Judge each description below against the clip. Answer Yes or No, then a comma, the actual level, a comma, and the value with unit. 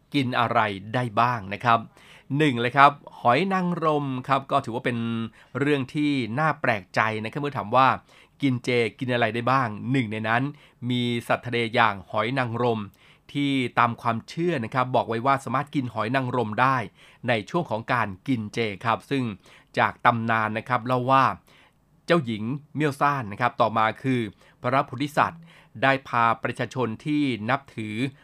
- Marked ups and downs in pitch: No, average, 3.4 semitones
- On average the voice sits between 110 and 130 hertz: Yes, low, 125 Hz